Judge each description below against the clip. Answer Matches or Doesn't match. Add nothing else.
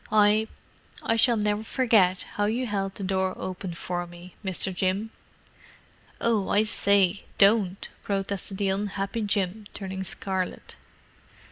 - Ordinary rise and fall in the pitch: Doesn't match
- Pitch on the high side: Matches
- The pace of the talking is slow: Matches